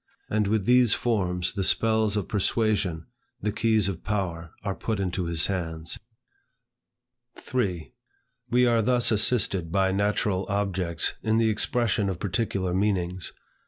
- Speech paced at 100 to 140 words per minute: Yes, slow, 135 wpm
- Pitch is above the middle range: No, low, 100 Hz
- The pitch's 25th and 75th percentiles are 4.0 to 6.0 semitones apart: No, average, 3.3 semitones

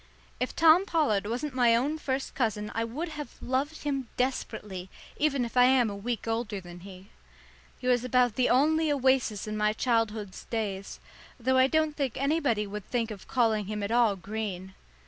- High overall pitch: Yes, high, 240 Hz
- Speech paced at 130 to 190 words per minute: Yes, average, 185 wpm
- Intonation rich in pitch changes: No, average, 4.1 semitones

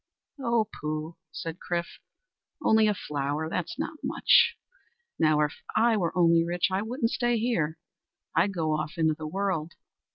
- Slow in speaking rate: No, average, 155 wpm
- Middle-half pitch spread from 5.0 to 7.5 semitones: Yes, wide, 5.4 semitones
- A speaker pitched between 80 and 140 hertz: No, medium, 170 Hz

